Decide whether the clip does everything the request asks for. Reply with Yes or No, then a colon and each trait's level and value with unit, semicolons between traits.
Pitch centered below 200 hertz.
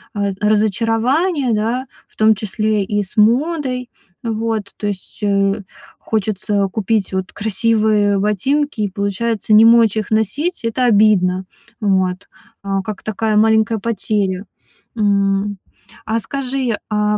No: high, 215 Hz